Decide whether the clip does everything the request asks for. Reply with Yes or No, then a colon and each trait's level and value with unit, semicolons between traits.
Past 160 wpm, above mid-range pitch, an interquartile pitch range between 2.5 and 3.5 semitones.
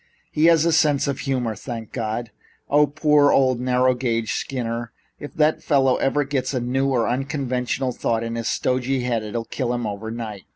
No: average, 180 wpm; low, 125 Hz; average, 3.0 semitones